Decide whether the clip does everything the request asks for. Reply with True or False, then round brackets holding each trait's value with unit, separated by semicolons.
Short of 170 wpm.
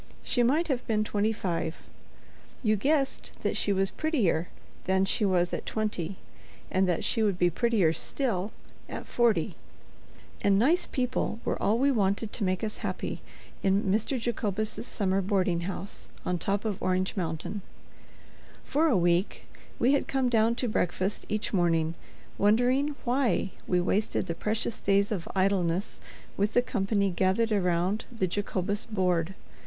True (155 wpm)